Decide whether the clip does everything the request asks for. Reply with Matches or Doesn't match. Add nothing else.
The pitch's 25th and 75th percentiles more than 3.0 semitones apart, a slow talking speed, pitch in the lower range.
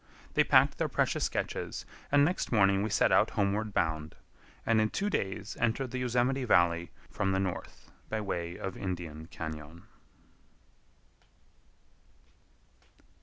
Matches